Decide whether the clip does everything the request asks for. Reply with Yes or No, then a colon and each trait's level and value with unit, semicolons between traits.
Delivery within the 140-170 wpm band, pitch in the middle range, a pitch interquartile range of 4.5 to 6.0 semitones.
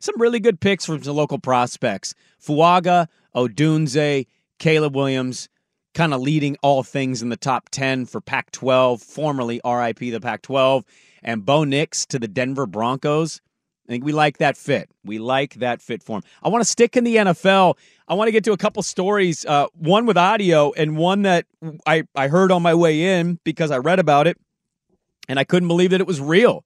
No: average, 200 wpm; medium, 155 Hz; wide, 5.4 semitones